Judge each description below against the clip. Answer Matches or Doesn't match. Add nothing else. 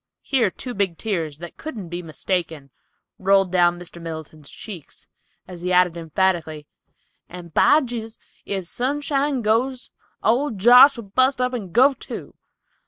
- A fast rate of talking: Doesn't match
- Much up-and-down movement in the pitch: Matches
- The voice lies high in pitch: Matches